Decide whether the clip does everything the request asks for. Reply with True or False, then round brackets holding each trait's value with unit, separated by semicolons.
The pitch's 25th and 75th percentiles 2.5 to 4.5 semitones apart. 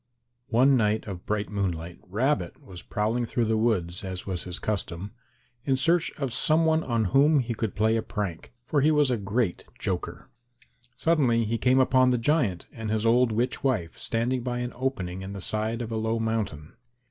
True (4.2 semitones)